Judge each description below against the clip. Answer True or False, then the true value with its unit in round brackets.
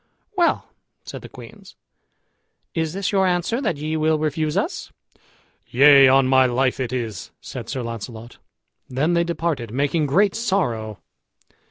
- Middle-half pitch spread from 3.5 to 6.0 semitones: True (5.1 semitones)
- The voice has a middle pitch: True (145 Hz)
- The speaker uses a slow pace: False (145 wpm)